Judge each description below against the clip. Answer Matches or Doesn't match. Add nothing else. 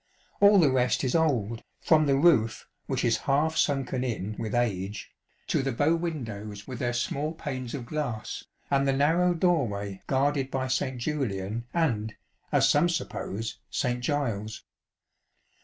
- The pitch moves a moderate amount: Matches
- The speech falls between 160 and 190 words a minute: Doesn't match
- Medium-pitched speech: Doesn't match